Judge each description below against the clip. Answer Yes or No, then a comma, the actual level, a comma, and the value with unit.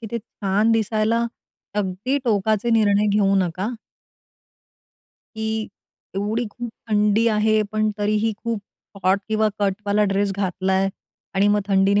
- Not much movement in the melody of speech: Yes, narrow, 1.7 semitones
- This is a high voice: Yes, high, 210 Hz